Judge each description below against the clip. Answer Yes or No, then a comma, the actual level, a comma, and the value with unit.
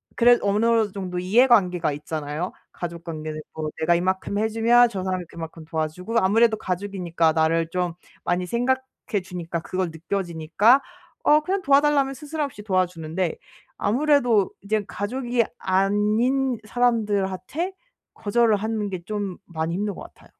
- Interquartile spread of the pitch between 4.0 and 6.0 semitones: Yes, average, 5.2 semitones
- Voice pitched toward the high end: Yes, high, 200 Hz